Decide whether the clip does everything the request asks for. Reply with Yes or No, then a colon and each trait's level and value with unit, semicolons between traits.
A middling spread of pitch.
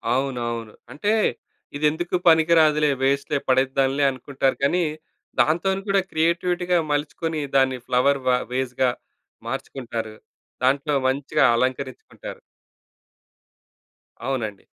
Yes: average, 3.5 semitones